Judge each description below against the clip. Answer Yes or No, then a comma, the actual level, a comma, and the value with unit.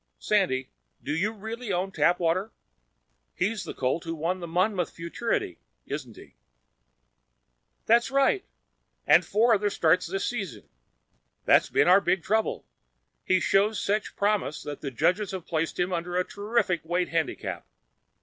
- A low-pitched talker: No, medium, 185 Hz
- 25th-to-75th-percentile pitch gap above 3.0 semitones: Yes, average, 4.0 semitones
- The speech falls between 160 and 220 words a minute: No, average, 145 wpm